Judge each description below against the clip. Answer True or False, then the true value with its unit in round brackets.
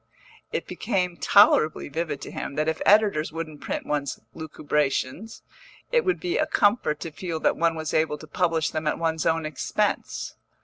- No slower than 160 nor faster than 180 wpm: True (175 wpm)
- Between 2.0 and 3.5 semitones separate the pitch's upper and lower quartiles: True (3.0 semitones)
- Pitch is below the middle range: False (160 Hz)